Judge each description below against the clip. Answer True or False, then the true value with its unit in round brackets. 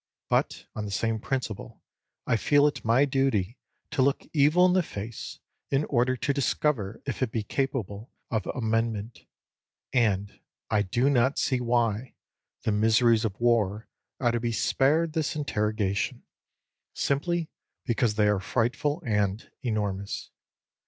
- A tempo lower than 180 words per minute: True (140 wpm)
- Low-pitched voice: True (115 Hz)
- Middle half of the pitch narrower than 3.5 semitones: False (4.3 semitones)